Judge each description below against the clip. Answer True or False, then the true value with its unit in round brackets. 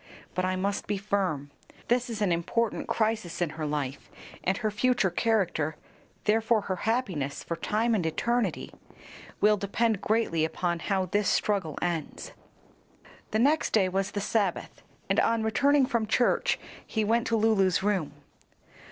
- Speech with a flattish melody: False (4.1 semitones)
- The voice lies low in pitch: False (205 Hz)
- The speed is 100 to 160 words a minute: True (150 wpm)